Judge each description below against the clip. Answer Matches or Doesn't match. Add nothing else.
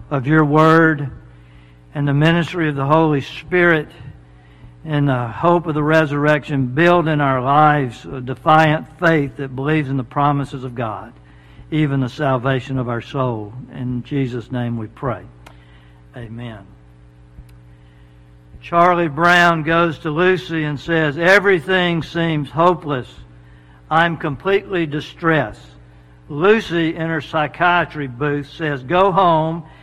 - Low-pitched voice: Doesn't match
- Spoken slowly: Matches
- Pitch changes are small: Doesn't match